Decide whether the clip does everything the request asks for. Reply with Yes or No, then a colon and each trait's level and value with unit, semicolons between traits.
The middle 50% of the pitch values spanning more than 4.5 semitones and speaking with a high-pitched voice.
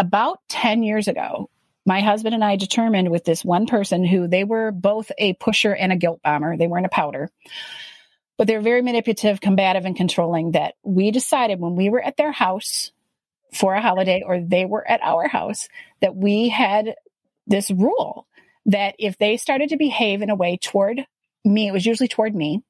No: average, 3.2 semitones; high, 205 Hz